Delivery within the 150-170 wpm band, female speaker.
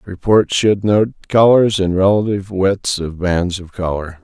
No: average, 155 wpm; male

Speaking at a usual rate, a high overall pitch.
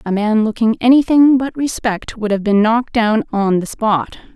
Yes: average, 195 wpm; high, 225 Hz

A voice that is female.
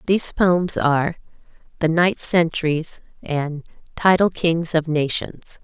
Yes: female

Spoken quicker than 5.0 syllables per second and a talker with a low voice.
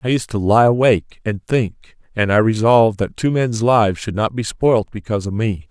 Yes: 5.2 syllables/s; low, 110 Hz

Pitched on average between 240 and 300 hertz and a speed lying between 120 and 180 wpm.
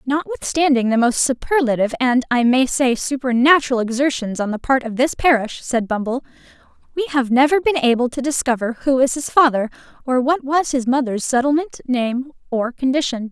Yes: very high, 260 Hz; average, 170 wpm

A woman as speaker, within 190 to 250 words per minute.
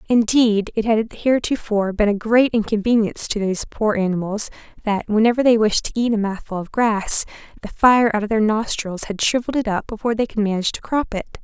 Yes: female; fast, 205 wpm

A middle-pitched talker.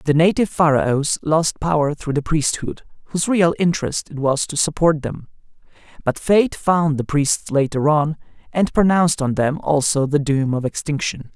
Yes: medium, 150 Hz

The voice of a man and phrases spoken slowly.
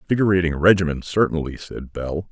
Yes: male; slow, 130 wpm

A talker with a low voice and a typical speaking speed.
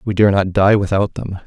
No: low, 100 Hz; fast, 245 wpm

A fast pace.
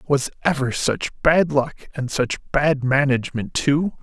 No: average, 150 wpm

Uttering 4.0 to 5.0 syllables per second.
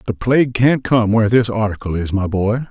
No: 5.5 syllables/s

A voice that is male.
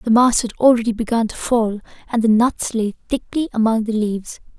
No: female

